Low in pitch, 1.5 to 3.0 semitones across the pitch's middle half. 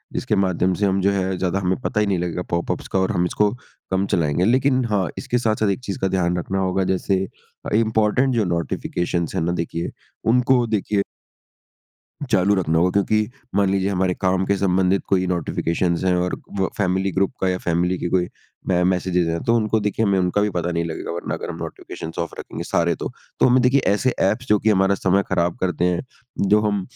Yes: very low, 95 Hz; average, 2.7 semitones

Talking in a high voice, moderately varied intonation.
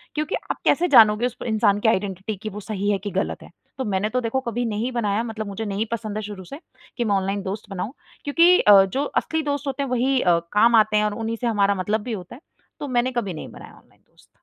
Yes: high, 215 Hz; average, 3.2 semitones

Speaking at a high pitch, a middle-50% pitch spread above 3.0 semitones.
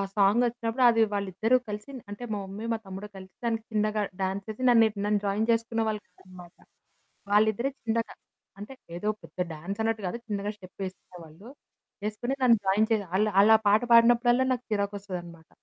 No: high, 210 Hz; narrow, 2.6 semitones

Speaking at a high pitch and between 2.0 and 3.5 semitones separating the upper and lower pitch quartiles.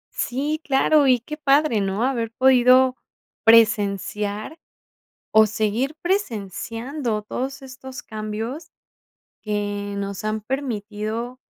No: high, 230 Hz; average, 4.0 semitones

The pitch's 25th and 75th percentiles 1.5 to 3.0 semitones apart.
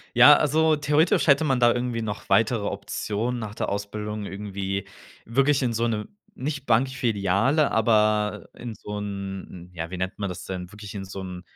No: average, 4.0 semitones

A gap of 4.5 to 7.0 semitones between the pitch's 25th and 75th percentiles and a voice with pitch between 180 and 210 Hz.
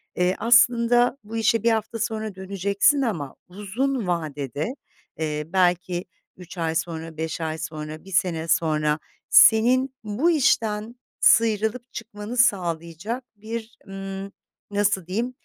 Yes: wide, 5.4 semitones; high, 200 Hz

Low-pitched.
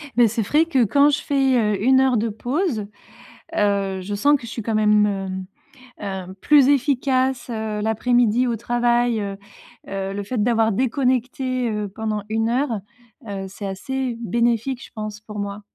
No: high, 230 Hz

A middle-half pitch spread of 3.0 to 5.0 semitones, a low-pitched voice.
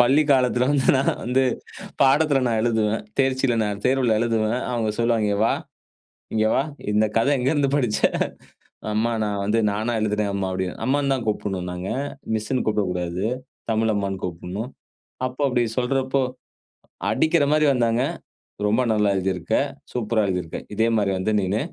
Yes: average, 3.9 semitones; low, 115 Hz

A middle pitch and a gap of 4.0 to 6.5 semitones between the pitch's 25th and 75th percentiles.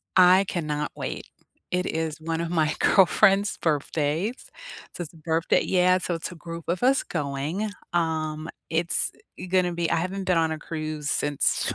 No: medium, 165 Hz; average, 2.7 semitones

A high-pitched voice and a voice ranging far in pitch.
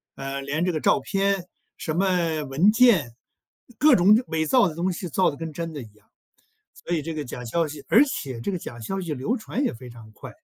No: medium, 165 Hz; wide, 5.8 semitones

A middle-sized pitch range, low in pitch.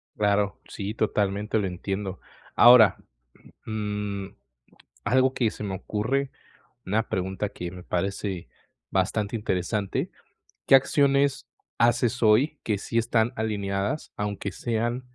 Yes: average, 3.2 semitones; low, 105 Hz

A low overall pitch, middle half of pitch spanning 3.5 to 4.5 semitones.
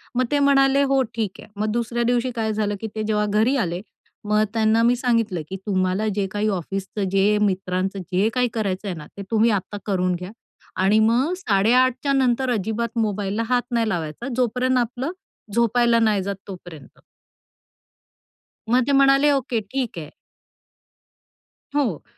No: high, 220 Hz; average, 4.0 semitones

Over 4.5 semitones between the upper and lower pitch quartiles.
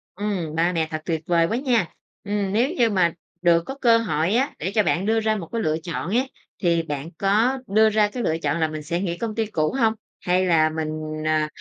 Yes: average, 5.2 semitones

